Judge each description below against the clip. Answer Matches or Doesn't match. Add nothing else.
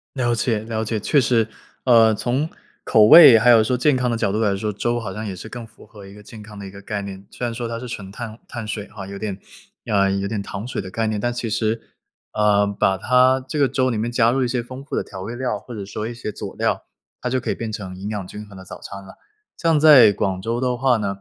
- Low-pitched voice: Matches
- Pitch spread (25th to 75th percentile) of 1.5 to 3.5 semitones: Matches